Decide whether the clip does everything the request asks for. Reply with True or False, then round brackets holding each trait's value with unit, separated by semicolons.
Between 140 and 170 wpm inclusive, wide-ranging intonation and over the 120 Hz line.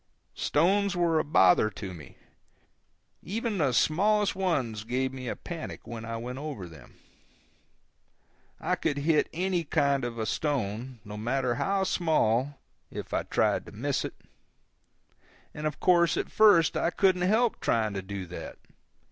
True (155 wpm; 7.4 semitones; 140 Hz)